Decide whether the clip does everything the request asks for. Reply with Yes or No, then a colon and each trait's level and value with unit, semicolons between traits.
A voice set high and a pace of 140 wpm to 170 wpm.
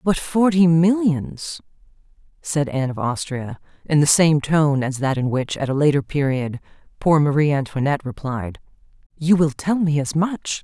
No: medium, 150 Hz; average, 165 wpm